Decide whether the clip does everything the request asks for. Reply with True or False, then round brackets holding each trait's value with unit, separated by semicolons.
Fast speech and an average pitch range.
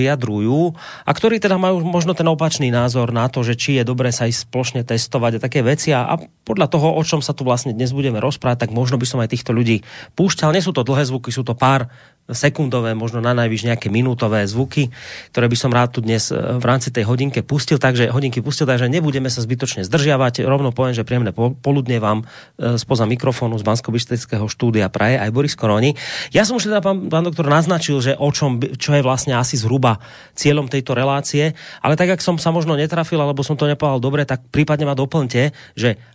True (210 wpm; 3.5 semitones)